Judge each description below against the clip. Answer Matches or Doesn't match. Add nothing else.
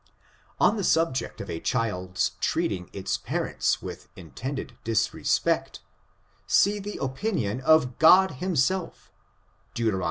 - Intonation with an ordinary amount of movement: Doesn't match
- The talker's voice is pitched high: Doesn't match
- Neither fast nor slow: Doesn't match